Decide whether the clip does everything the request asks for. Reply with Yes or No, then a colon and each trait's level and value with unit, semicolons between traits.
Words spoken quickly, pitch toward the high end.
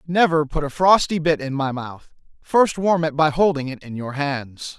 No: fast, 215 wpm; medium, 150 Hz